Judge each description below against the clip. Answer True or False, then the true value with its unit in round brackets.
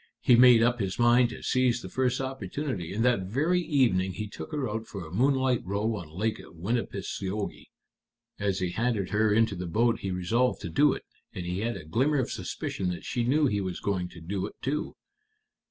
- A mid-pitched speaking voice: False (110 Hz)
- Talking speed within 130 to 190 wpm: False (205 wpm)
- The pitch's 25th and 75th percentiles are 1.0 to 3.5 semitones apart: False (4.9 semitones)